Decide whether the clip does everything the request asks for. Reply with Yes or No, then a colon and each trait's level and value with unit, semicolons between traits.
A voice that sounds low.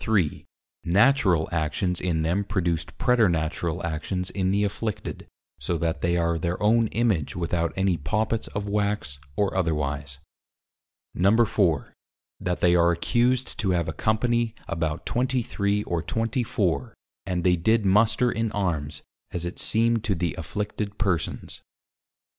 Yes: very low, 95 Hz